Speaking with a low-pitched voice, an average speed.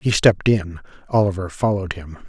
Yes: very low, 95 Hz; average, 160 wpm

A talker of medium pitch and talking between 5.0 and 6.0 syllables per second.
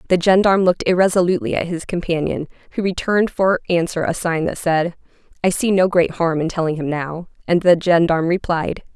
Yes: medium, 175 Hz; 5.9 syllables/s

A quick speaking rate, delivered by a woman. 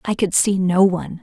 Yes: fast, 245 wpm; female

